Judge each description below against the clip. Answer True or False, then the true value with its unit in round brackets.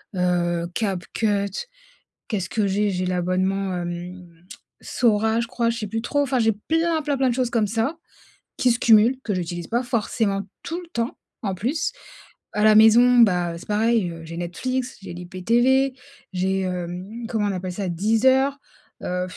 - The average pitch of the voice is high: True (210 Hz)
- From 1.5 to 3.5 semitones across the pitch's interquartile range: False (4.7 semitones)